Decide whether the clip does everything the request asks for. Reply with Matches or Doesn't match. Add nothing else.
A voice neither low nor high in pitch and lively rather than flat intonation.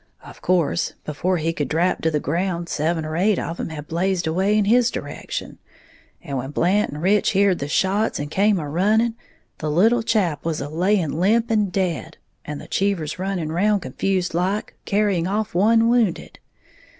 Doesn't match